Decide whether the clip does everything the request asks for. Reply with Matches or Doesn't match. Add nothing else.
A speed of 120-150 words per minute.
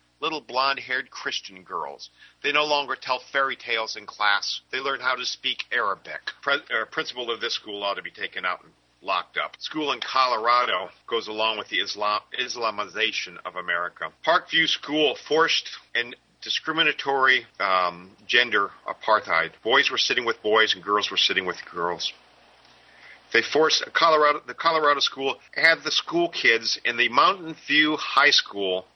Doesn't match